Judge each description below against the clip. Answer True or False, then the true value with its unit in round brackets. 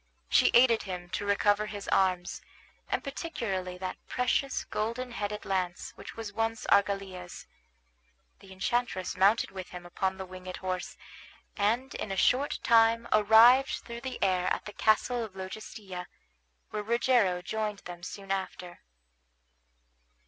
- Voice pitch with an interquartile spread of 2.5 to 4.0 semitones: True (3.5 semitones)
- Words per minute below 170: True (140 wpm)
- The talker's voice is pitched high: True (205 Hz)